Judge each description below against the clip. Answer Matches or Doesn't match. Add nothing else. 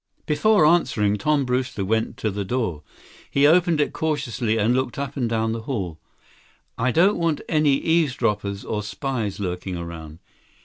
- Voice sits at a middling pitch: Doesn't match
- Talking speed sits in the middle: Matches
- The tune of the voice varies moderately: Doesn't match